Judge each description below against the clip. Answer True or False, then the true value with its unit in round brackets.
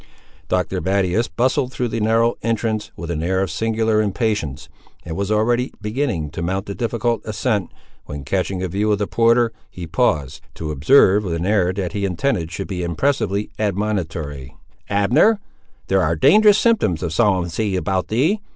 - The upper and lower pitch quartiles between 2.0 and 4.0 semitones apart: False (4.7 semitones)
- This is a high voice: False (100 Hz)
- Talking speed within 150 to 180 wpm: True (170 wpm)